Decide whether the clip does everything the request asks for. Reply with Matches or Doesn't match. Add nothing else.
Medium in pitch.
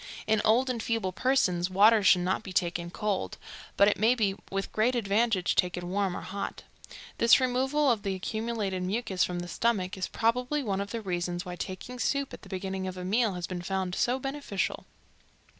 Doesn't match